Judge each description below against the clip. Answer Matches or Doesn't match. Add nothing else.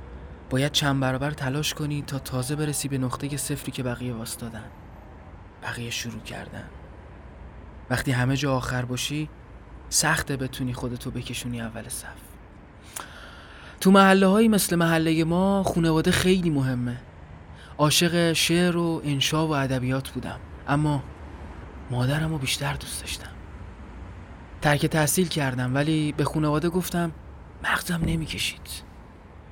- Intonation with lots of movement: Matches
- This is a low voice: Matches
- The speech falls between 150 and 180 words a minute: Doesn't match